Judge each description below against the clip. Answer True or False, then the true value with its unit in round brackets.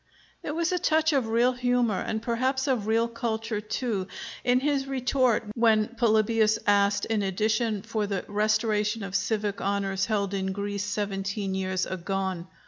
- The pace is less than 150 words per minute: False (155 wpm)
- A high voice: True (215 Hz)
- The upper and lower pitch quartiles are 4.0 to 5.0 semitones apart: False (2.9 semitones)